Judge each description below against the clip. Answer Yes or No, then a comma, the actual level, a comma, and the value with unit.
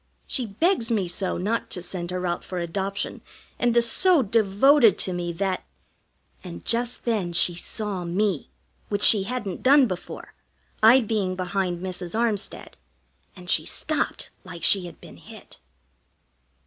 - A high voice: Yes, high, 195 Hz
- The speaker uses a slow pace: No, average, 155 wpm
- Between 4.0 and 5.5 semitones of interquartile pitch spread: Yes, average, 4.4 semitones